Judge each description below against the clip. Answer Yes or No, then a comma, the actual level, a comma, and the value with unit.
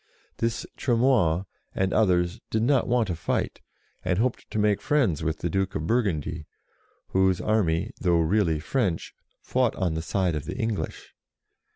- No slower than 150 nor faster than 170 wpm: Yes, average, 160 wpm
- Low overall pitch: Yes, very low, 95 Hz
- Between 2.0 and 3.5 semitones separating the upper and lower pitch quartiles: No, average, 5.3 semitones